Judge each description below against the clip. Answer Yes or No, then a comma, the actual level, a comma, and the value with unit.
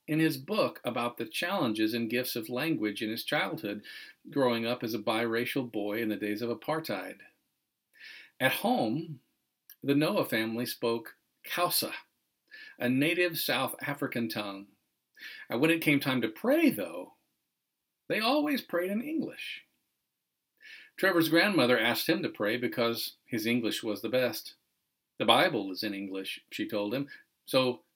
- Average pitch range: No, wide, 6.6 semitones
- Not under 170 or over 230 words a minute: No, average, 150 wpm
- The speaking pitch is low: Yes, low, 125 Hz